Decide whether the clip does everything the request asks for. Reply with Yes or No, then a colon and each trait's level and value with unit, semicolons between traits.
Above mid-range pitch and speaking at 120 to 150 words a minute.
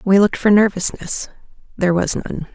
Yes: high, 195 Hz; average, 140 wpm